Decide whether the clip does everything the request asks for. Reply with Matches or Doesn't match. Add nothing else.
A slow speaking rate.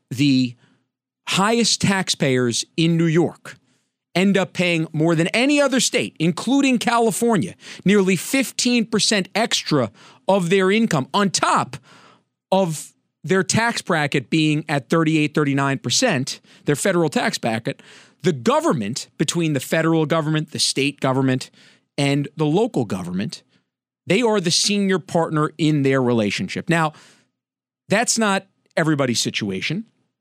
Matches